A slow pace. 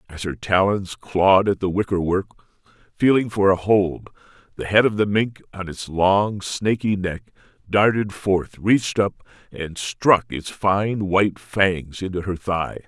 No: average, 160 wpm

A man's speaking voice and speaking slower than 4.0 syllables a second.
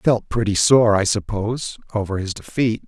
No: male; 4.9 syllables/s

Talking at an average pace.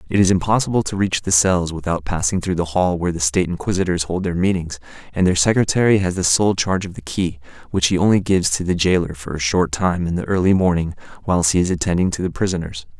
No: fast, 235 wpm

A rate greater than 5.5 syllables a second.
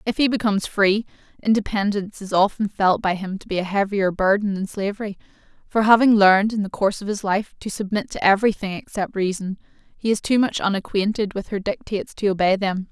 Yes: 6.0 syllables/s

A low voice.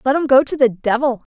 No: very high, 260 Hz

